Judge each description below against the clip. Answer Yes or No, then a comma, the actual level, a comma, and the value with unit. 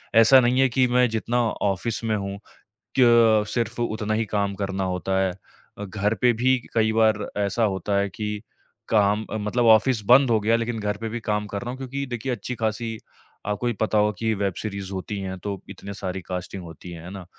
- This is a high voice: No, low, 110 Hz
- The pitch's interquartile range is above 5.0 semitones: No, average, 2.9 semitones